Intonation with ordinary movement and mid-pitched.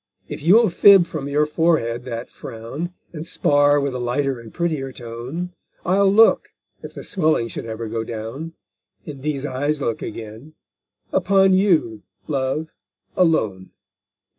No: wide, 6.2 semitones; medium, 145 Hz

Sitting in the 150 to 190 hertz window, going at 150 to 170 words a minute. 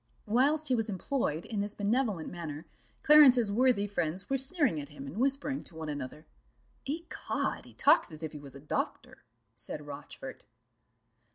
No: high, 205 Hz; average, 165 wpm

